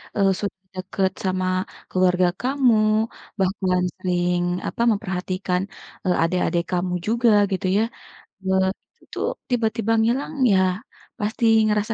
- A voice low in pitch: No, high, 190 Hz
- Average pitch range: Yes, average, 3.2 semitones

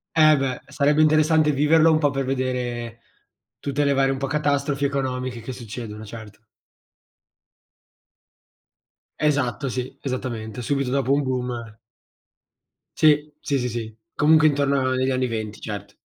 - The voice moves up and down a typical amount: Yes, average, 3.0 semitones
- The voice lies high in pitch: No, low, 135 Hz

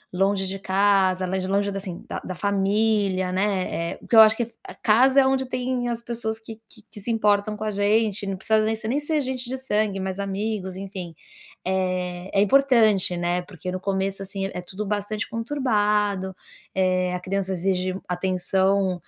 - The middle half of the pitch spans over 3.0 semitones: No, average, 2.7 semitones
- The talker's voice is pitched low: No, high, 200 Hz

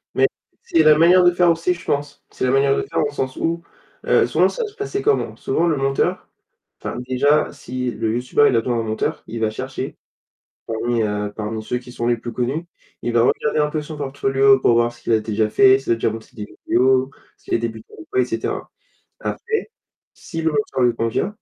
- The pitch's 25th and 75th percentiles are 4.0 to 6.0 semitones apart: Yes, average, 4.6 semitones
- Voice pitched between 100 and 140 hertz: Yes, low, 130 Hz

